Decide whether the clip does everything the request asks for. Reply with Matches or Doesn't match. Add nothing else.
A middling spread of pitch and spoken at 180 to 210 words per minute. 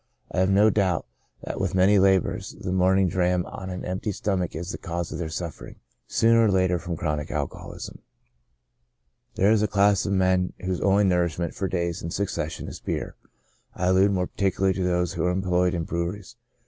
Doesn't match